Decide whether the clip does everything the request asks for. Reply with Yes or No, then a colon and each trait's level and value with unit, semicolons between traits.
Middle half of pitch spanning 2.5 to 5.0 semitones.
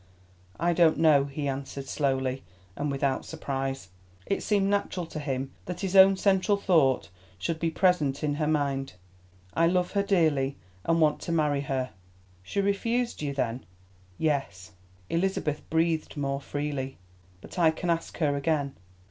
Yes: average, 4.1 semitones